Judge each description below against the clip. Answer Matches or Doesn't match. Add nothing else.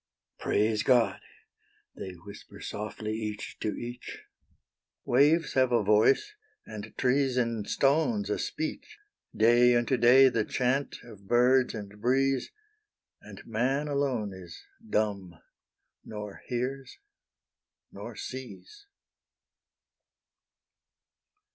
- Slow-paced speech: Matches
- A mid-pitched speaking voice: Doesn't match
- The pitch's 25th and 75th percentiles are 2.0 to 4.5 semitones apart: Matches